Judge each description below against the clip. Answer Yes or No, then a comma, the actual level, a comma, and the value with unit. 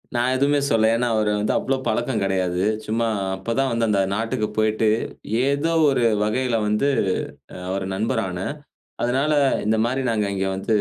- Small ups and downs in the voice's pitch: No, average, 3.4 semitones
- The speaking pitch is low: Yes, low, 115 Hz